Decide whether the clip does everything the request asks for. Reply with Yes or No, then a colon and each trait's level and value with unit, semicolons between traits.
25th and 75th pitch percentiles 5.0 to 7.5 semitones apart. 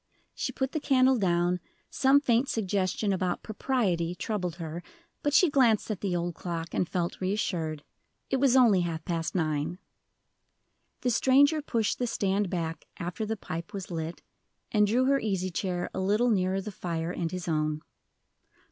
Yes: average, 5.3 semitones